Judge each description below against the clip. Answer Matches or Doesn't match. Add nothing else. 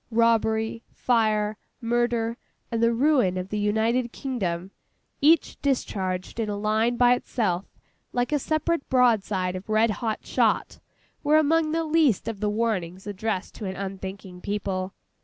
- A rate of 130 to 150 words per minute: Matches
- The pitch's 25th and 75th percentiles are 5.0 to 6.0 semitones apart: Doesn't match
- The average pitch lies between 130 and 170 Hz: Doesn't match